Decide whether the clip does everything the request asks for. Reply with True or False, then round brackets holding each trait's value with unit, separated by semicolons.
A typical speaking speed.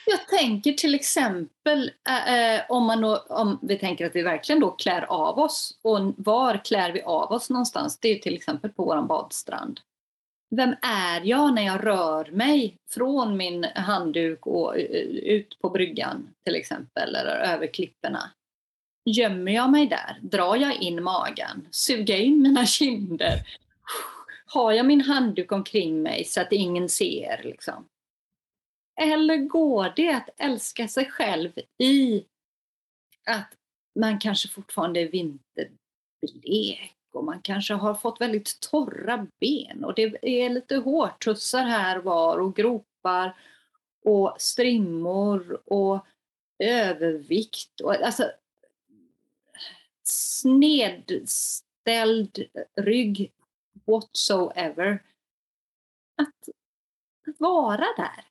False (120 wpm)